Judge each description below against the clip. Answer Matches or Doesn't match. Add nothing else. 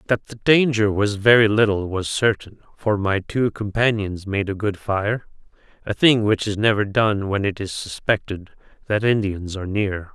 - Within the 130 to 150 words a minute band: Doesn't match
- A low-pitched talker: Matches